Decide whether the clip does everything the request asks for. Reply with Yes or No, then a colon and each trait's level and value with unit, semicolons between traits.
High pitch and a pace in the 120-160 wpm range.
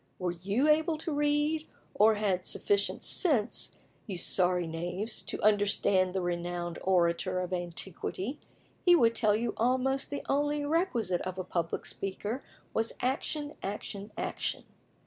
Yes: high, 205 Hz; average, 145 wpm